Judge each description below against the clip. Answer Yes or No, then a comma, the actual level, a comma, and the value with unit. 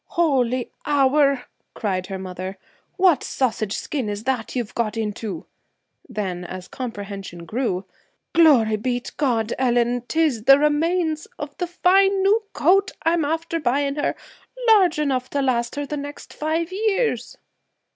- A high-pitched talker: Yes, very high, 270 Hz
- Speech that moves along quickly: No, average, 145 wpm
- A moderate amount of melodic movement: No, wide, 6.4 semitones